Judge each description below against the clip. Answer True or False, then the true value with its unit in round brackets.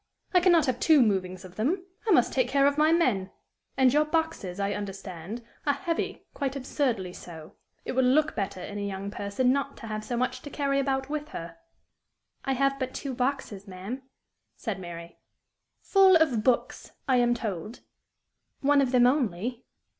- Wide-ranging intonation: True (5.8 semitones)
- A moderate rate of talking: True (185 wpm)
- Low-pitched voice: False (250 Hz)